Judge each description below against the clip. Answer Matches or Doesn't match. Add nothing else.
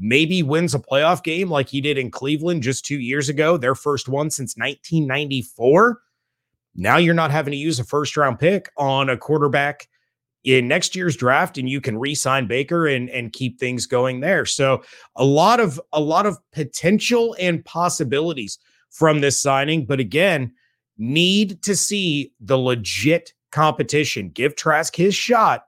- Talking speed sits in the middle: Matches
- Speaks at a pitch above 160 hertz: Doesn't match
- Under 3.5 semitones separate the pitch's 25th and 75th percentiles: Doesn't match